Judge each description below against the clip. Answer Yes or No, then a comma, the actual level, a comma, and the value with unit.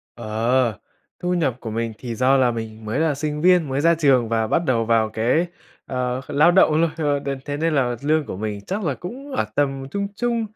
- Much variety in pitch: Yes, wide, 5.7 semitones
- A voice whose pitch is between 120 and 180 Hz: Yes, low, 135 Hz